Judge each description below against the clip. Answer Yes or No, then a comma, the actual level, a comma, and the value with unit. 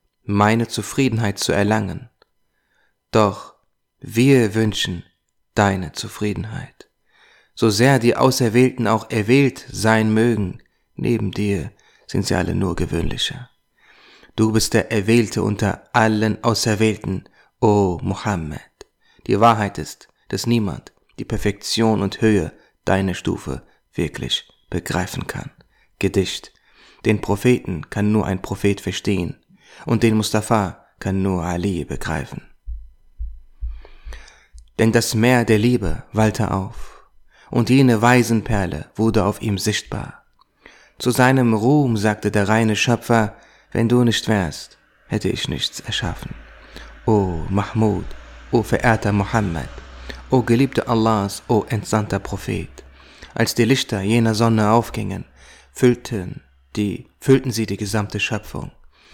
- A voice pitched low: Yes, low, 110 Hz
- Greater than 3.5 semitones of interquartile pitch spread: No, average, 2.9 semitones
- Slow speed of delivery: Yes, slow, 120 wpm